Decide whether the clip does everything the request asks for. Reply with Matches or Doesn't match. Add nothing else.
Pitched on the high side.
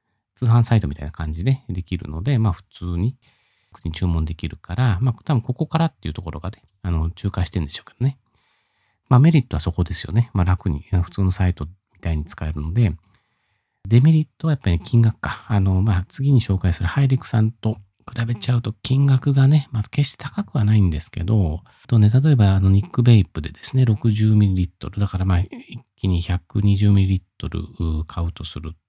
Doesn't match